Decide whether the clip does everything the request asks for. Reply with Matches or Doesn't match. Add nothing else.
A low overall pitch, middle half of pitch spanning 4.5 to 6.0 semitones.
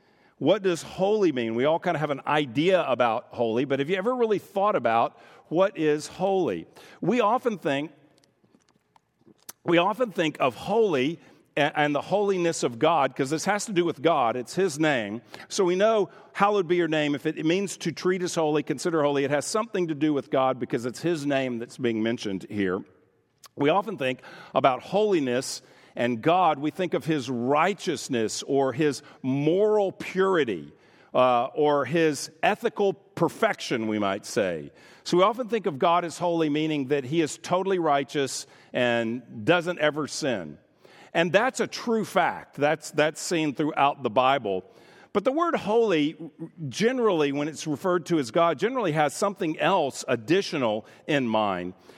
Doesn't match